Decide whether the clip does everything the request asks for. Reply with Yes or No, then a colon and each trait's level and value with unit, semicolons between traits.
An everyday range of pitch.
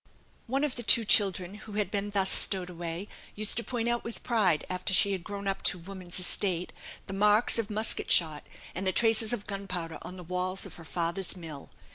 Yes: average, 3.0 semitones